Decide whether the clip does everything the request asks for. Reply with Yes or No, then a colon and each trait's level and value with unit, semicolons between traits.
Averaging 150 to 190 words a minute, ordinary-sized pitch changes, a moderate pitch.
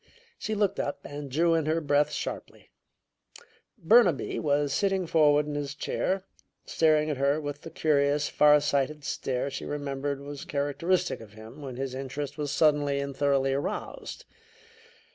No: average, 155 wpm; narrow, 1.9 semitones; medium, 145 Hz